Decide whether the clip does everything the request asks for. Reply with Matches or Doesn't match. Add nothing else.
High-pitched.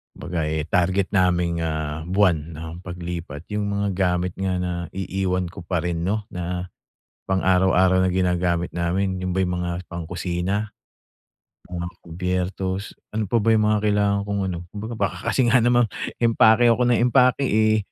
Doesn't match